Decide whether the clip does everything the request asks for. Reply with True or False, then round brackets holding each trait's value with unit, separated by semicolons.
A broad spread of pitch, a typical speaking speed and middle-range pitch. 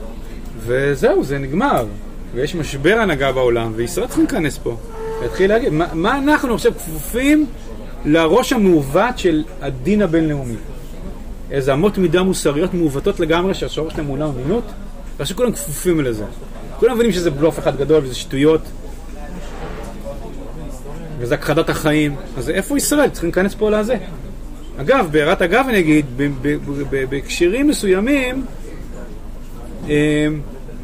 True (7.1 semitones; 125 wpm; 160 Hz)